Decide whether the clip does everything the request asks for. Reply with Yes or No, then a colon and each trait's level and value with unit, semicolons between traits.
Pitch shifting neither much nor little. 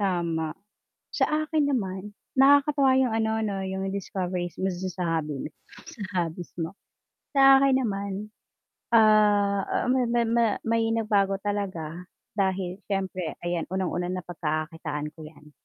Yes: average, 4.2 semitones